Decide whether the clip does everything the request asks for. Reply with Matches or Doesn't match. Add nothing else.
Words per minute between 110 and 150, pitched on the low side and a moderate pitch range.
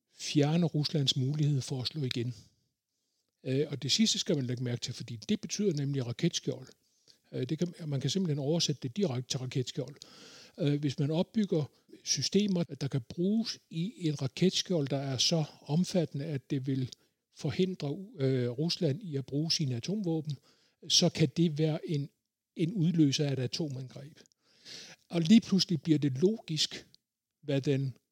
Doesn't match